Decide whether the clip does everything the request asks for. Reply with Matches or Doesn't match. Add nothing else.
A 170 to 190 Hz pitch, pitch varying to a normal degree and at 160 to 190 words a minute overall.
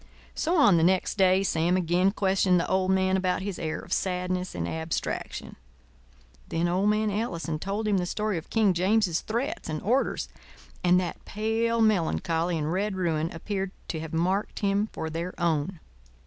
Matches